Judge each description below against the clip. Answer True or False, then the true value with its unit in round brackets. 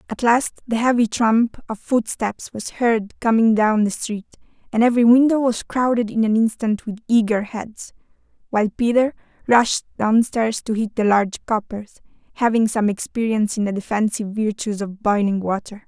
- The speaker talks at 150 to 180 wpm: True (165 wpm)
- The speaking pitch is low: False (220 Hz)